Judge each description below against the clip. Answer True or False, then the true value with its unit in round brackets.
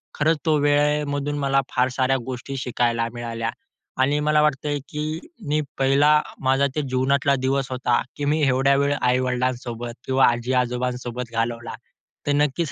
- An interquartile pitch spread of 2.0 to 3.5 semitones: True (2.8 semitones)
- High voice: False (135 Hz)